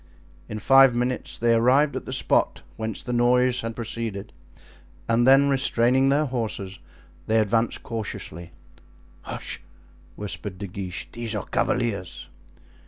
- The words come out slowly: Yes, slow, 130 wpm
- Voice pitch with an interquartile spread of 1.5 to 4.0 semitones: Yes, average, 3.0 semitones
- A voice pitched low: Yes, low, 115 Hz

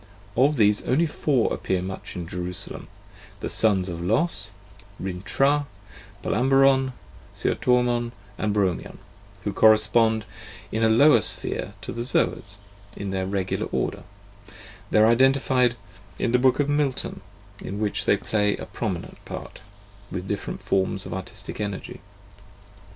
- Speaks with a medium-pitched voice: No, low, 110 Hz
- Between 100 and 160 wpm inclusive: Yes, average, 140 wpm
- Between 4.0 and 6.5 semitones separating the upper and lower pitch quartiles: Yes, average, 4.9 semitones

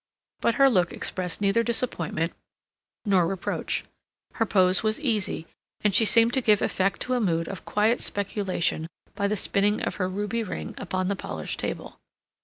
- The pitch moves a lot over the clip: No, average, 3.4 semitones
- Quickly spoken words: No, average, 170 wpm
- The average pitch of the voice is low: No, high, 200 Hz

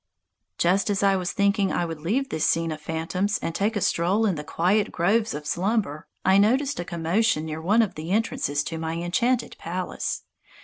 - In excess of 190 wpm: Yes, average, 200 wpm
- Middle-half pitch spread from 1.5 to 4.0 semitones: No, average, 4.4 semitones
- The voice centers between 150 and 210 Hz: Yes, medium, 185 Hz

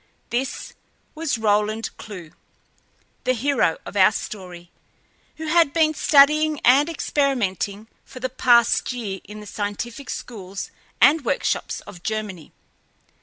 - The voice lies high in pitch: Yes, high, 235 Hz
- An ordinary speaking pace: No, slow, 120 wpm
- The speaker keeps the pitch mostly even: No, wide, 5.6 semitones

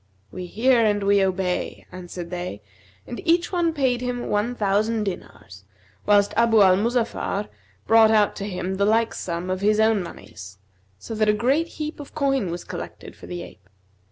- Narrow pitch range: No, average, 4.3 semitones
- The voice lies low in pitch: No, high, 210 Hz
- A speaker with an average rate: Yes, average, 180 wpm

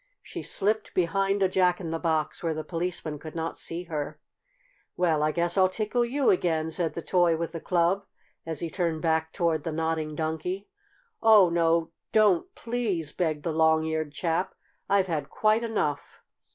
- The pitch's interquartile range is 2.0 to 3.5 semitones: Yes, average, 2.8 semitones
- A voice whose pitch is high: No, medium, 170 Hz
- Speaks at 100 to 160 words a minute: No, average, 180 wpm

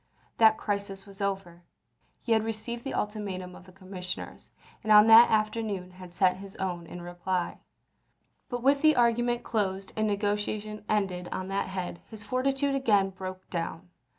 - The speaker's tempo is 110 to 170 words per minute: Yes, average, 160 wpm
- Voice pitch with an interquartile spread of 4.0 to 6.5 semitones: No, average, 3.0 semitones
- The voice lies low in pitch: No, high, 200 Hz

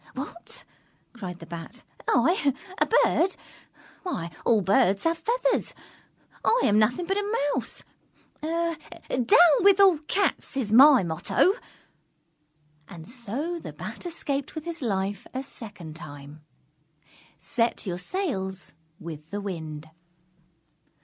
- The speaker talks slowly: Yes, slow, 120 wpm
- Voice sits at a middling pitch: No, high, 235 Hz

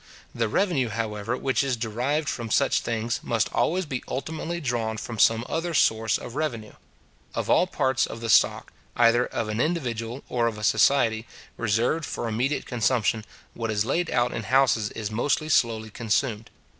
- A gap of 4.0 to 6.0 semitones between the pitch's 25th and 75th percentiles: No, average, 3.5 semitones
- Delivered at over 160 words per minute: Yes, average, 170 wpm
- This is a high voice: No, low, 120 Hz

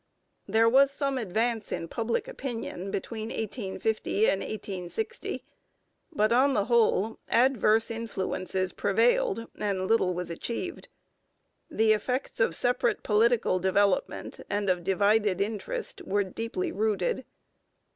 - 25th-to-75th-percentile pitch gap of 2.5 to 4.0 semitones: Yes, average, 3.5 semitones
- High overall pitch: Yes, high, 220 Hz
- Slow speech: Yes, slow, 115 wpm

